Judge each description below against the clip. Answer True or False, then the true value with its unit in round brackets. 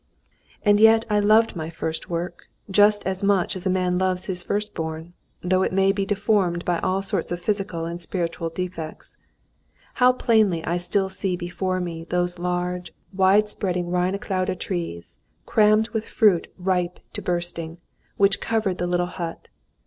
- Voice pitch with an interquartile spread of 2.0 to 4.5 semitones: True (2.4 semitones)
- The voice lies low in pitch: False (185 Hz)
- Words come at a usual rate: True (165 wpm)